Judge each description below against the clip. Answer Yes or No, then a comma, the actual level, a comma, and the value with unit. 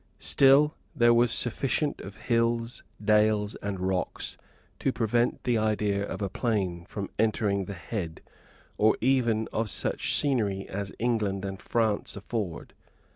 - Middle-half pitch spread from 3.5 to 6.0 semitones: No, average, 3.0 semitones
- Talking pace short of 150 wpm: Yes, slow, 135 wpm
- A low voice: Yes, low, 110 Hz